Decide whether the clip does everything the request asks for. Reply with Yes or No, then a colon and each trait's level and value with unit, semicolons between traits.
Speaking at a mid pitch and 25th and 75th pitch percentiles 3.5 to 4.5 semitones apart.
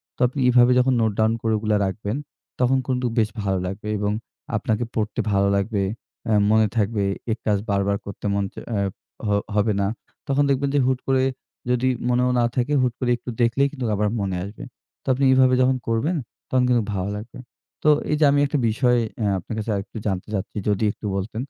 No: low, 110 Hz; average, 3.8 semitones